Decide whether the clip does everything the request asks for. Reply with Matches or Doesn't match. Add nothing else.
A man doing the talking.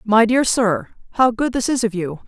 Doesn't match